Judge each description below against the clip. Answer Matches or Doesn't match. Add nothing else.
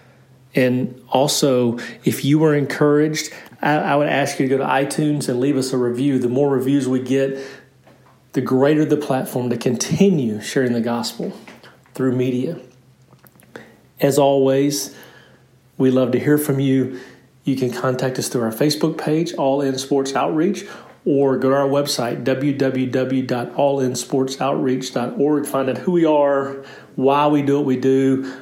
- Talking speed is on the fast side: Doesn't match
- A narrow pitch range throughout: Matches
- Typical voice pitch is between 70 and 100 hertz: Doesn't match